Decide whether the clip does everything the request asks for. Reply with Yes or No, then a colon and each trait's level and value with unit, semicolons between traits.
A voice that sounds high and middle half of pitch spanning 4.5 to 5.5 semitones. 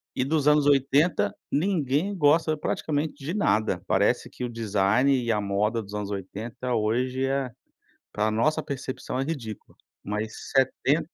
No: low, 130 Hz; average, 5.2 semitones